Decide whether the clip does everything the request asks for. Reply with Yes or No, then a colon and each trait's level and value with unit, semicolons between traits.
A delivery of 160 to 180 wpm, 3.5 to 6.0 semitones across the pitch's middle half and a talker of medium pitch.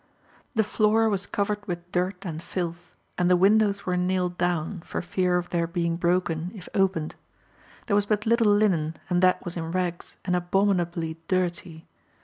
No: average, 170 wpm; narrow, 2.5 semitones; medium, 180 Hz